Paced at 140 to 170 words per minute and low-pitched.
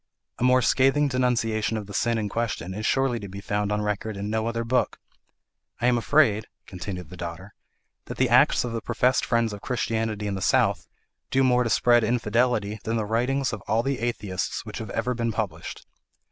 No: average, 200 wpm; low, 115 Hz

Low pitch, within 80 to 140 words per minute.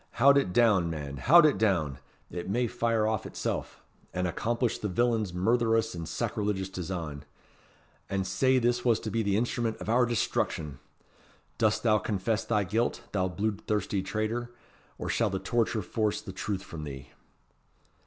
No: low, 105 Hz; average, 165 wpm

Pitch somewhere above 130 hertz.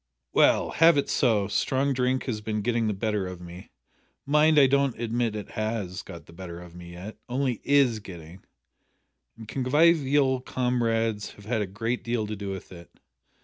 No: low, 115 Hz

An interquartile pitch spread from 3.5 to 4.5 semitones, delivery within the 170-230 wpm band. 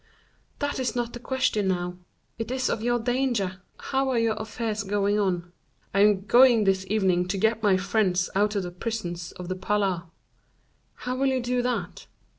Yes: average, 4.2 semitones; average, 185 wpm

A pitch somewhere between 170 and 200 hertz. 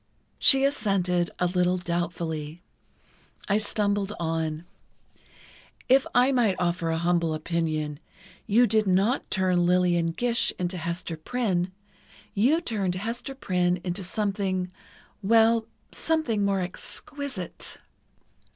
Yes: medium, 185 Hz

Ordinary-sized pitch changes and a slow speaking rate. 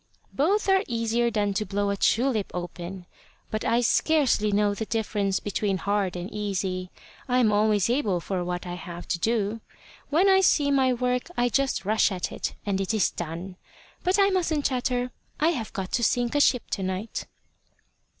No: average, 4.6 semitones; average, 185 wpm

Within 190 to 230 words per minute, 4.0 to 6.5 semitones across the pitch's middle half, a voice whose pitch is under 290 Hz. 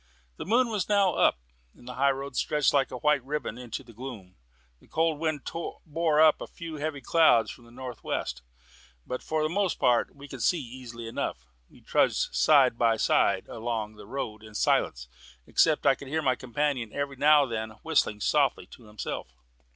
Yes: average, 195 wpm; average, 4.7 semitones; low, 135 Hz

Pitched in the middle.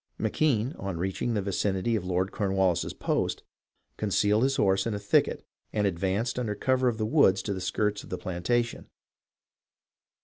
No: low, 105 Hz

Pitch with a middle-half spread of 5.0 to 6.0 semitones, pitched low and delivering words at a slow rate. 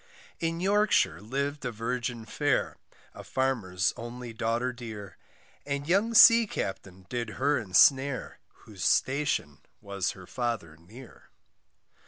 Yes: wide, 5.6 semitones; low, 120 Hz; slow, 120 wpm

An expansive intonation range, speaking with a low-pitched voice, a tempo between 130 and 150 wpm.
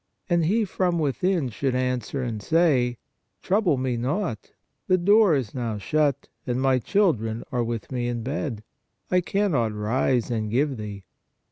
No: wide, 6.3 semitones; low, 130 Hz; average, 160 wpm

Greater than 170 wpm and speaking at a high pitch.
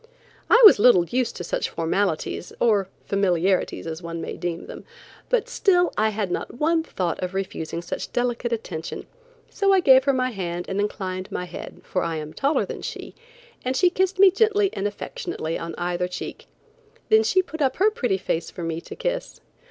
Yes: average, 190 wpm; high, 205 Hz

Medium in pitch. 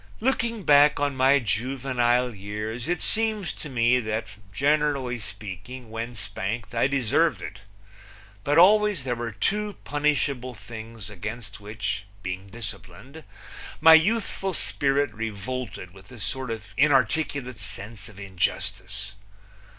No: low, 120 Hz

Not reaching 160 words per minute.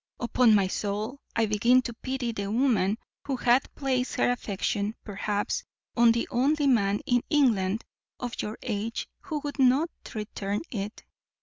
Yes: average, 150 wpm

